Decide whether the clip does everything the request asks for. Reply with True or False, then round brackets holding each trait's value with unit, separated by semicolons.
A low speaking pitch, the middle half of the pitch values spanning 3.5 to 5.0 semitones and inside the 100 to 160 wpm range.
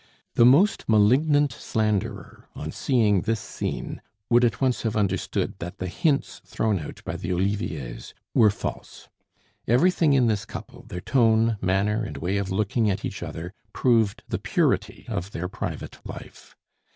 True (110 Hz; 4.0 semitones; 155 wpm)